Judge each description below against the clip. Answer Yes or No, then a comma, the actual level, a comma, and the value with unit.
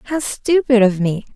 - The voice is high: Yes, high, 240 Hz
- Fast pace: No, average, 175 wpm